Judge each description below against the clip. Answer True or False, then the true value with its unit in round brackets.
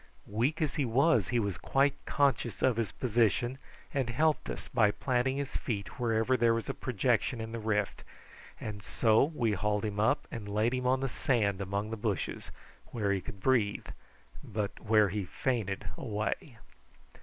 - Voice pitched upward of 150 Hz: False (115 Hz)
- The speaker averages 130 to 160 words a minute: False (175 wpm)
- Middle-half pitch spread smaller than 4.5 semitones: True (3.6 semitones)